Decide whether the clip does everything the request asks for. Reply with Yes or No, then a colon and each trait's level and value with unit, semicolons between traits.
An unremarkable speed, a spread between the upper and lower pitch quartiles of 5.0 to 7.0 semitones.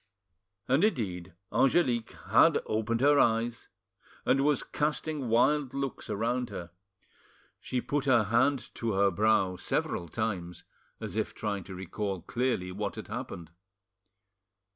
No: slow, 130 wpm; wide, 5.4 semitones